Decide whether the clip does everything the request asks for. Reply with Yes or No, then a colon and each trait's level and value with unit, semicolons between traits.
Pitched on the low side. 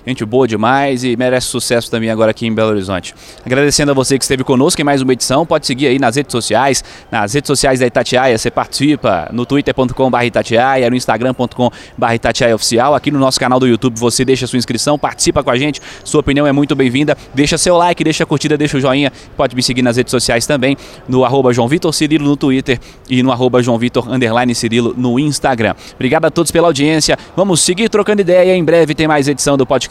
Yes: low, 130 Hz